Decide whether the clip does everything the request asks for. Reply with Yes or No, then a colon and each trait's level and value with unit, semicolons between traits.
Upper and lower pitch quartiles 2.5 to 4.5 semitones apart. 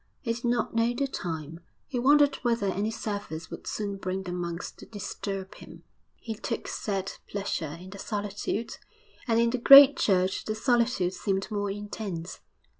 Yes: average, 3.6 semitones